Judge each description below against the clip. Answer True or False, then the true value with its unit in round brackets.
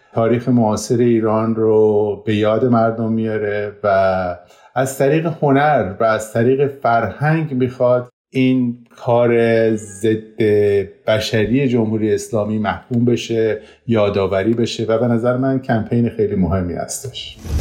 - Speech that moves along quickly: False (120 wpm)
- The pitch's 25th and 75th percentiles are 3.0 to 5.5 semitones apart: False (2.4 semitones)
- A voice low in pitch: True (115 Hz)